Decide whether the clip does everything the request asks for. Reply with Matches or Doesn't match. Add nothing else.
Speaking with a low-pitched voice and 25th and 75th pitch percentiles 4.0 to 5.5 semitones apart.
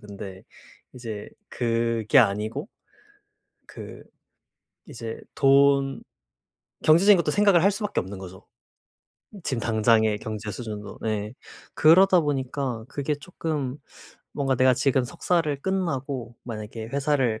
Matches